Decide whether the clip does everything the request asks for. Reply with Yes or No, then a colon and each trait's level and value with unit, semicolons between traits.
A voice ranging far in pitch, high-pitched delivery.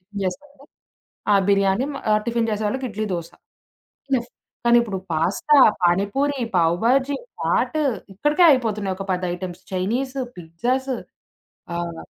Yes: wide, 6.1 semitones; high, 215 Hz